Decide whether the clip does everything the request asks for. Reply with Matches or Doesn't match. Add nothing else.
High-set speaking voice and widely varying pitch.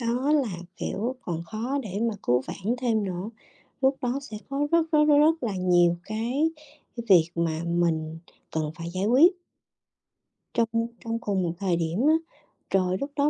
Matches